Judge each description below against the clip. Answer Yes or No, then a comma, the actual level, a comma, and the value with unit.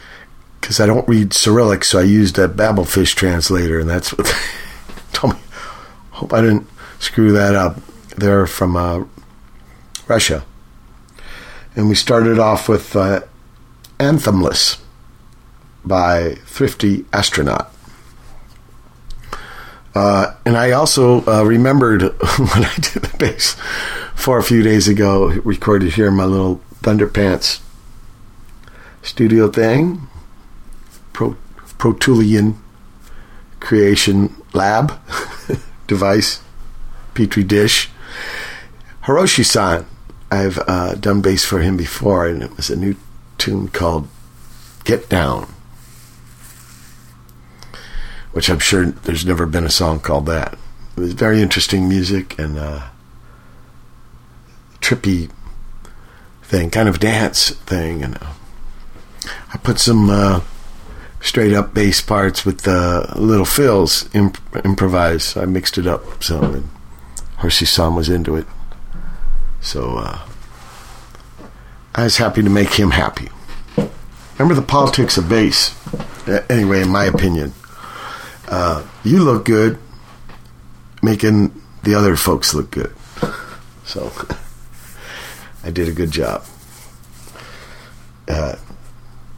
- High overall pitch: No, low, 100 Hz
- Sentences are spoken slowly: Yes, slow, 115 wpm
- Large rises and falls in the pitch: No, average, 3.9 semitones